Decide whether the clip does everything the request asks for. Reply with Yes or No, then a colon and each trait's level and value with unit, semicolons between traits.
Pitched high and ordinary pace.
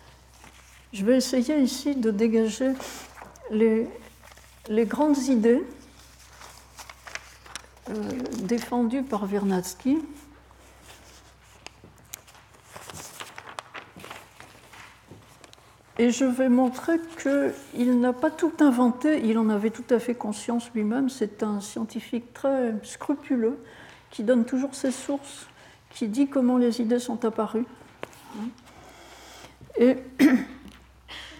No: high, 245 Hz; slow, 95 wpm